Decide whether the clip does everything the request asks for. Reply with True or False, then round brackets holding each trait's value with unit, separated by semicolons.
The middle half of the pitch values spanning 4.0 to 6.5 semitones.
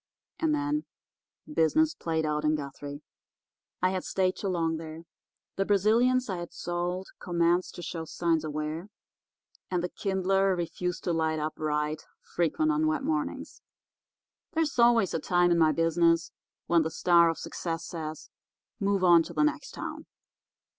False (3.4 semitones)